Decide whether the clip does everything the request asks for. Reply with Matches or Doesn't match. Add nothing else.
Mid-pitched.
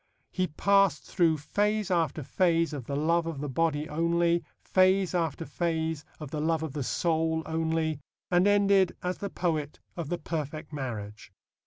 Matches